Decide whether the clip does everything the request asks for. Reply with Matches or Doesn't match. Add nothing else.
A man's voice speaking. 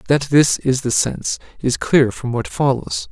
Matches